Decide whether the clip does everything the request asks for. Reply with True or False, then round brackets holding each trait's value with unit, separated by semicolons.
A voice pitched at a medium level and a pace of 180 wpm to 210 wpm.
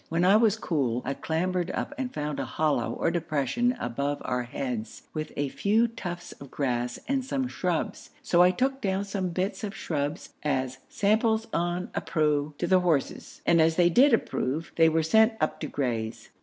True (165 Hz; 185 wpm)